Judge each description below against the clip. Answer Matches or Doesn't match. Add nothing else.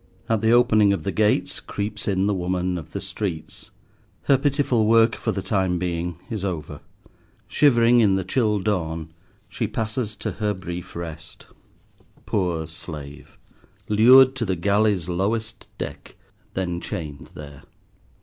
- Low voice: Matches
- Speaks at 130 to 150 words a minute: Matches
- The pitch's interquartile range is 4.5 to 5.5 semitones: Doesn't match